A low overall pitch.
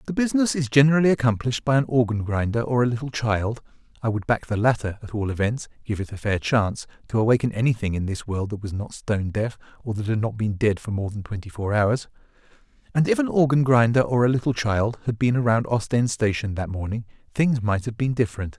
Yes: low, 115 Hz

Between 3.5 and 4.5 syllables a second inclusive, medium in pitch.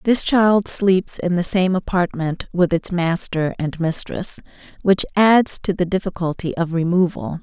Yes: 4.2 syllables/s; medium, 180 Hz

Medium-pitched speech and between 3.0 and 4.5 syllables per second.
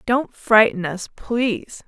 No: high, 220 Hz; 3.6 syllables/s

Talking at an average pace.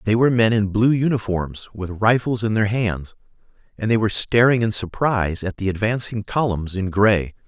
Yes: average, 185 wpm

